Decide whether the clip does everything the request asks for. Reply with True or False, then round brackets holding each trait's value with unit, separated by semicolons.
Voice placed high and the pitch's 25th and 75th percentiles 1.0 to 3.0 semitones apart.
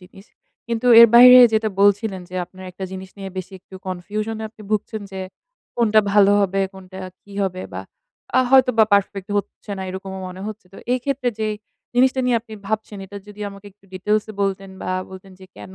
True (205 Hz; 2.5 semitones)